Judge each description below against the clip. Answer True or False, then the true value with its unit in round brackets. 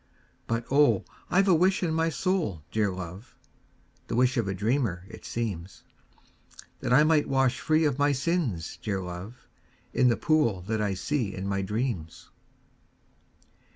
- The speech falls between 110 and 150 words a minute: False (160 wpm)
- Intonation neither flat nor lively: False (7.4 semitones)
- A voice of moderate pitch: False (120 Hz)